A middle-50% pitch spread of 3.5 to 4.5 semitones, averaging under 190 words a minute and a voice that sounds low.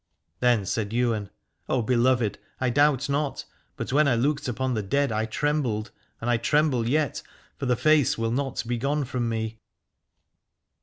Yes: average, 3.8 semitones; average, 165 wpm; low, 125 Hz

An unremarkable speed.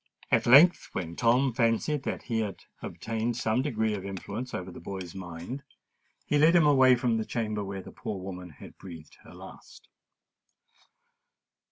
Yes: average, 165 wpm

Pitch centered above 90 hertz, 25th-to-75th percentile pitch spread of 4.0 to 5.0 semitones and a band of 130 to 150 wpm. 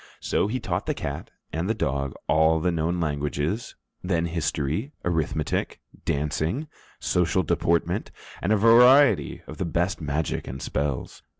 No: very low, 80 Hz; average, 4.5 semitones; average, 140 wpm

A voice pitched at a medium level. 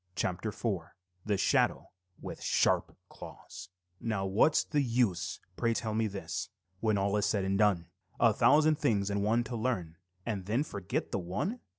No: low, 105 Hz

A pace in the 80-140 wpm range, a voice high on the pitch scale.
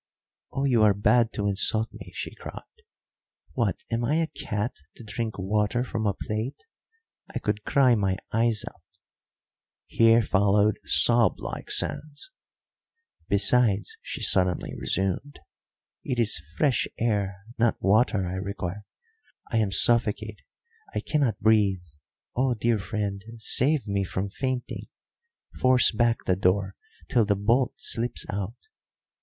No: slow, 135 wpm; low, 110 Hz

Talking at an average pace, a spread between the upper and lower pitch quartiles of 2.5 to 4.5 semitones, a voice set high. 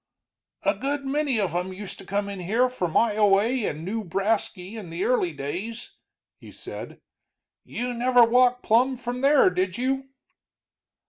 No: average, 150 wpm; average, 4.9 semitones; high, 225 Hz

